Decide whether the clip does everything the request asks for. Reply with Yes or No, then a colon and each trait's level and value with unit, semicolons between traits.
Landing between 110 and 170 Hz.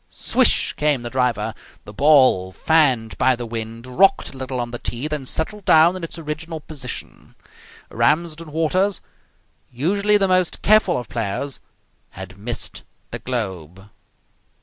Yes: low, 135 Hz